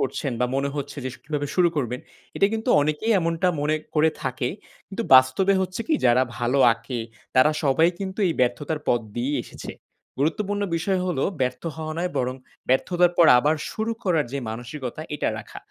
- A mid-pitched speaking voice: Yes, medium, 150 Hz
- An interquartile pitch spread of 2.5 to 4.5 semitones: No, wide, 5.4 semitones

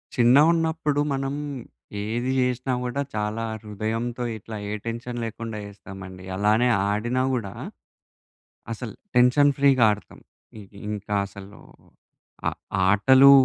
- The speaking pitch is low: Yes, low, 115 Hz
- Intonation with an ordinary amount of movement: Yes, average, 3.6 semitones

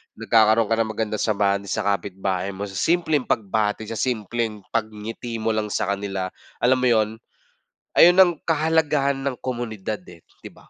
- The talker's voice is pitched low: Yes, low, 110 Hz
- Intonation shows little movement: No, average, 3.6 semitones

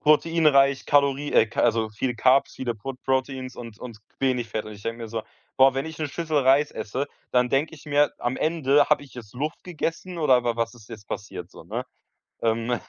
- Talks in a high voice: No, low, 130 Hz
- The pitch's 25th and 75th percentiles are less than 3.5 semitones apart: No, average, 3.8 semitones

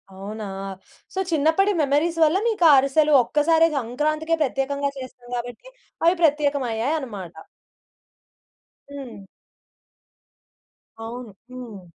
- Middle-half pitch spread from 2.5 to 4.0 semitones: No, average, 4.5 semitones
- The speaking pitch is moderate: No, very high, 280 Hz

